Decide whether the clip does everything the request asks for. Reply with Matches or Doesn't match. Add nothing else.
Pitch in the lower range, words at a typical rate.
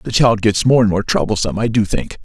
Doesn't match